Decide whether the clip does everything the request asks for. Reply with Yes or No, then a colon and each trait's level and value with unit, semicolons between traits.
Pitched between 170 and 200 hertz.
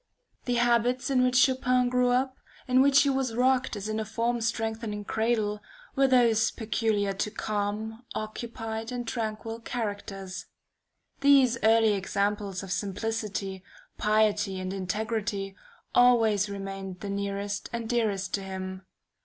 No: high, 220 Hz